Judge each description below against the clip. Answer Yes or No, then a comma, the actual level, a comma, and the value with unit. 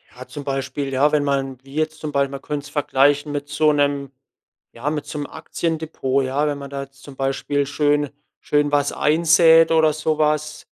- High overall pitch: No, medium, 145 Hz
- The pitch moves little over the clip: Yes, narrow, 1.7 semitones